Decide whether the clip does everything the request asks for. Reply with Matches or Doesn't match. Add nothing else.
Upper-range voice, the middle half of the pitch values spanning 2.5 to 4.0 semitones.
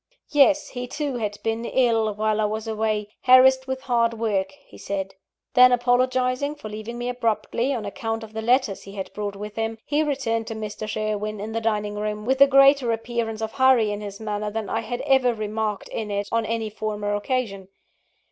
Matches